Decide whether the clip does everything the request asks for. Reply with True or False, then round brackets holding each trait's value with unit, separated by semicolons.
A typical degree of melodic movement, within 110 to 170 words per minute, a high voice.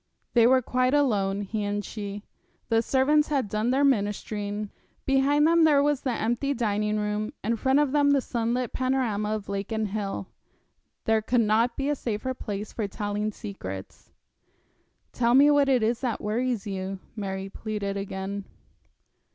True (4.1 semitones; 165 wpm; 220 Hz)